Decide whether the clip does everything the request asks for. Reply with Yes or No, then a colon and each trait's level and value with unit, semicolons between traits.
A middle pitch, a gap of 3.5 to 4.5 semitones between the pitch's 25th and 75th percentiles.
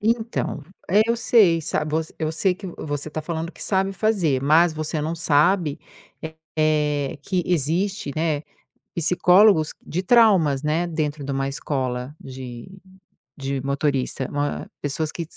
Yes: medium, 155 Hz; average, 3.8 semitones